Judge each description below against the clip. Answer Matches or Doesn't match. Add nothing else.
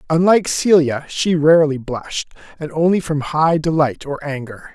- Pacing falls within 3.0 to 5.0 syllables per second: Matches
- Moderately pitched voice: Matches